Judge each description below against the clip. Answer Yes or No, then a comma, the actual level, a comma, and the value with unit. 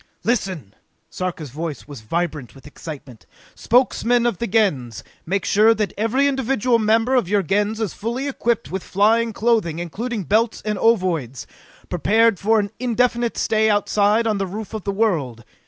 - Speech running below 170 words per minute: Yes, average, 160 wpm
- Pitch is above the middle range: Yes, high, 210 Hz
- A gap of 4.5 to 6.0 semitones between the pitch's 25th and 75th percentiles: Yes, average, 4.8 semitones